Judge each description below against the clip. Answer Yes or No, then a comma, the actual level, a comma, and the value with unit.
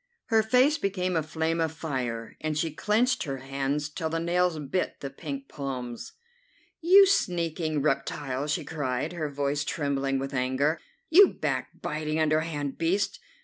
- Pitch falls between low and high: Yes, medium, 155 Hz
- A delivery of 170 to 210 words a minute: No, average, 145 wpm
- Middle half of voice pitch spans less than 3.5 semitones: No, average, 3.9 semitones